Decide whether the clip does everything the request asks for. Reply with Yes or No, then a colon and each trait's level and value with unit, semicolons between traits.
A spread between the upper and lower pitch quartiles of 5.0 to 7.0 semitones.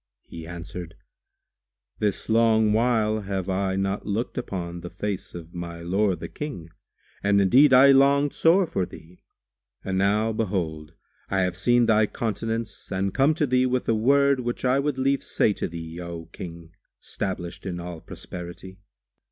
Yes: wide, 5.5 semitones